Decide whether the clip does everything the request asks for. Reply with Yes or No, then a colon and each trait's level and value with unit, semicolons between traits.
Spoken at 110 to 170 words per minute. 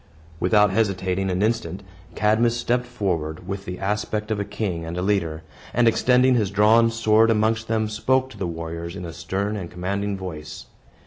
No: average, 180 wpm